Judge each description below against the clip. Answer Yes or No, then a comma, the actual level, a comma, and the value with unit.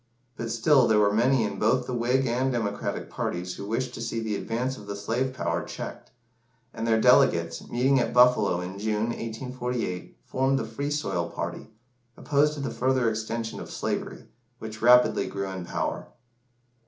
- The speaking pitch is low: Yes, low, 115 Hz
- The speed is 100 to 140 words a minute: No, average, 175 wpm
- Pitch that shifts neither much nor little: Yes, average, 3.4 semitones